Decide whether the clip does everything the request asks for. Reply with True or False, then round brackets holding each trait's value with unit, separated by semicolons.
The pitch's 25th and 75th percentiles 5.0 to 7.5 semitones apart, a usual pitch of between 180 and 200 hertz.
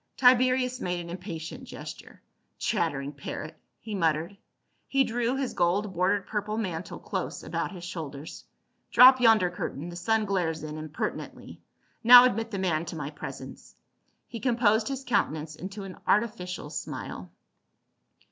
True (5.6 semitones; 190 Hz)